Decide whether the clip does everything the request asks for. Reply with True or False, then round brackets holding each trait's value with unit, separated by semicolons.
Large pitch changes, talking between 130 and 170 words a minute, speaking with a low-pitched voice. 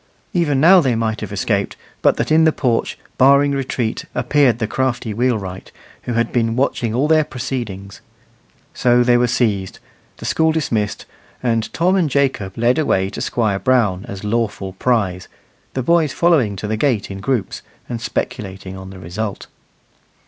False (4.8 semitones; 165 wpm; 120 Hz)